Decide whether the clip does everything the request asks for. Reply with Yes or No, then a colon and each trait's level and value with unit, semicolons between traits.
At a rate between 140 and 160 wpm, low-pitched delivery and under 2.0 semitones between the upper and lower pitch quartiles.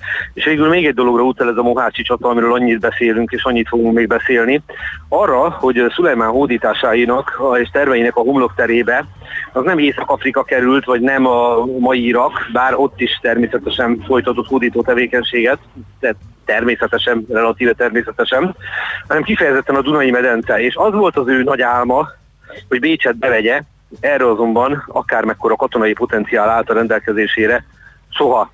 Yes: average, 150 wpm; low, 120 Hz; narrow, 1.3 semitones